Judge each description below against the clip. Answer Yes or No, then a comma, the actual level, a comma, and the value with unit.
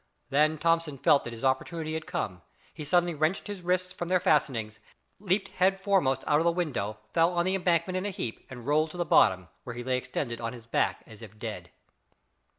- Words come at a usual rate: No, fast, 215 wpm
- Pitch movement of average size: No, wide, 6.4 semitones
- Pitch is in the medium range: Yes, medium, 155 Hz